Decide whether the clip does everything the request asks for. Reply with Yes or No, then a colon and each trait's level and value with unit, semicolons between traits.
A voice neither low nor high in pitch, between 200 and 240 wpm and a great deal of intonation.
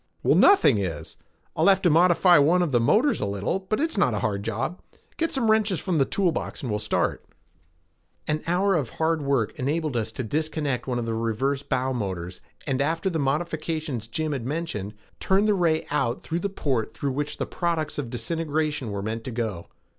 Yes: medium, 145 Hz; fast, 205 wpm; wide, 6.5 semitones